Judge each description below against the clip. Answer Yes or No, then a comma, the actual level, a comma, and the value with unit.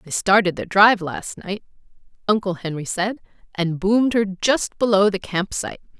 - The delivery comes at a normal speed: Yes, average, 160 wpm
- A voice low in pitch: No, high, 200 Hz